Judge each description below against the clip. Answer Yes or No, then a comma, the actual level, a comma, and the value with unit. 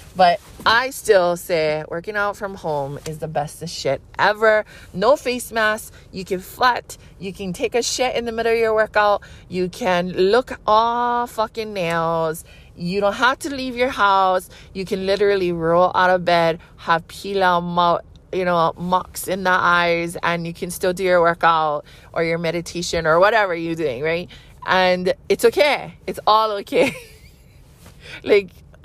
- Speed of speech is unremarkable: Yes, average, 170 wpm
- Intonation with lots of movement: No, average, 4.2 semitones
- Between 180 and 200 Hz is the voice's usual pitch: Yes, medium, 185 Hz